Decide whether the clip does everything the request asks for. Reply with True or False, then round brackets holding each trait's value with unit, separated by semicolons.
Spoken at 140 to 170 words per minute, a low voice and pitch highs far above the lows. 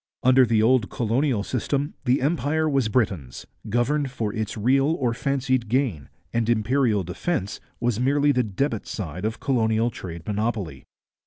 False (150 wpm; 120 Hz; 4.1 semitones)